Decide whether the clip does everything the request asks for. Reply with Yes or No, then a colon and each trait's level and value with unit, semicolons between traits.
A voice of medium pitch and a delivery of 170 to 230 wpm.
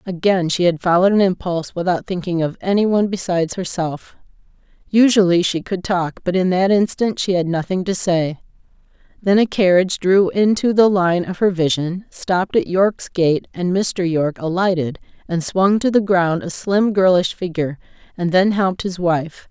Yes: medium, 180 Hz; average, 180 wpm